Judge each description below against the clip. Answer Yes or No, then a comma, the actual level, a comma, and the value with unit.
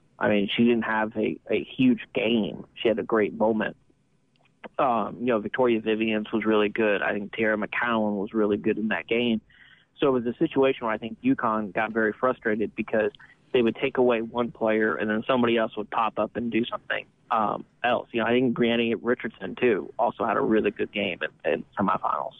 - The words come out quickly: Yes, fast, 210 wpm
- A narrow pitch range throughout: Yes, narrow, 1.9 semitones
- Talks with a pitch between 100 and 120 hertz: Yes, low, 110 Hz